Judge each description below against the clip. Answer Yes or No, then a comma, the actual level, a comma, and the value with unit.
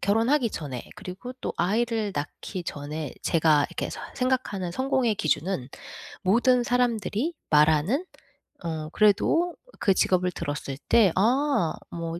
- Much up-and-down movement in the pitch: Yes, wide, 7.3 semitones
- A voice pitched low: No, high, 195 Hz